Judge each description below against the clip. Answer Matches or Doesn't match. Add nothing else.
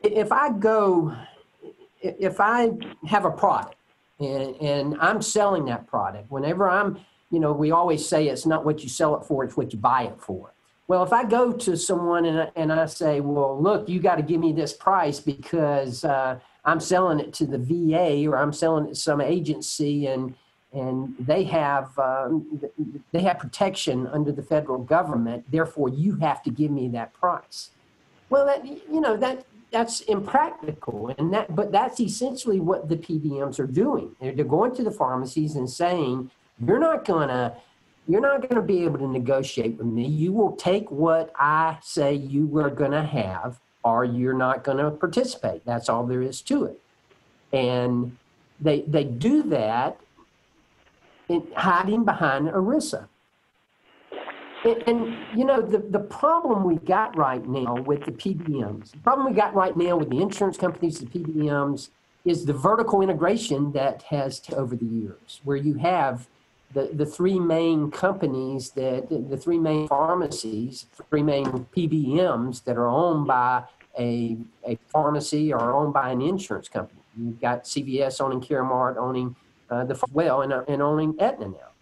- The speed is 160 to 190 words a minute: Matches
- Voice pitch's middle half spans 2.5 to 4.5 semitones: Doesn't match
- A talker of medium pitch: Matches